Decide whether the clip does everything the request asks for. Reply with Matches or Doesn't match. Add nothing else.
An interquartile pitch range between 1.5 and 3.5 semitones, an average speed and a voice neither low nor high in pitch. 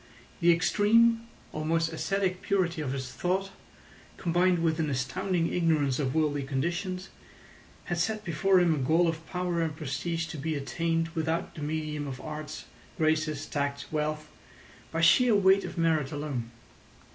Matches